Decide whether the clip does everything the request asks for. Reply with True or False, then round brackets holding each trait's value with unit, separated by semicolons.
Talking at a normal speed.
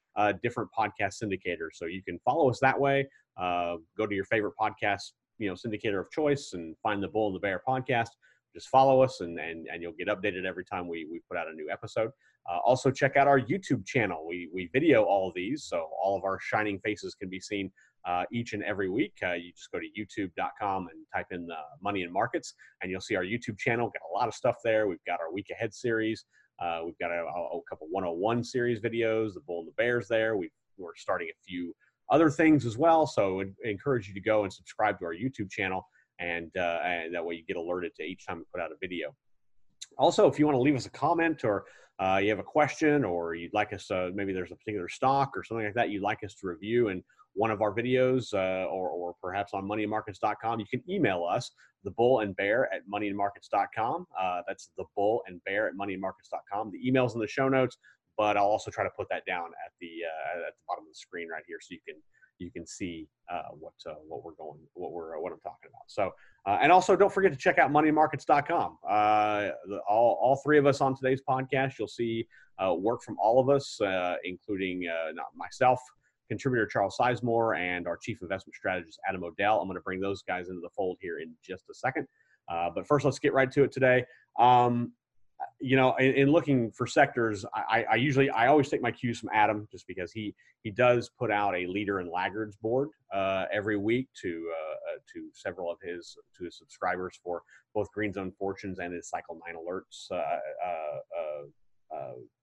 False (225 wpm)